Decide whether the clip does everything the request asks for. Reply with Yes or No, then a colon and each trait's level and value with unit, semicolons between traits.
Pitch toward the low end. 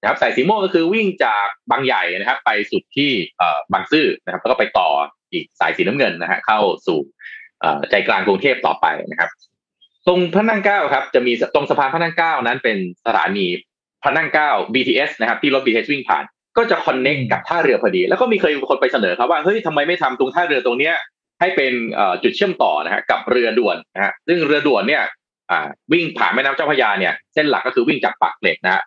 No: medium, 180 Hz